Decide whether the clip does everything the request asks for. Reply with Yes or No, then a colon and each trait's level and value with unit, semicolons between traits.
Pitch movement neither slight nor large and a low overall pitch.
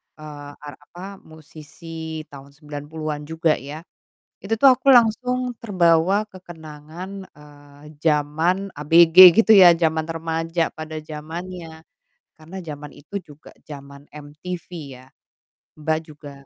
No: average, 3.3 semitones; medium, 160 Hz